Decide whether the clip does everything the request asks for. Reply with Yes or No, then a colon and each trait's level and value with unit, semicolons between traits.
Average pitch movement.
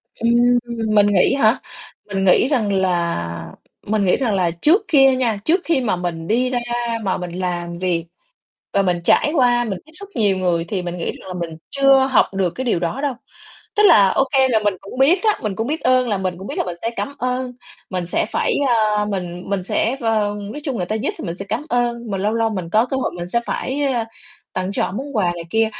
No: wide, 5.8 semitones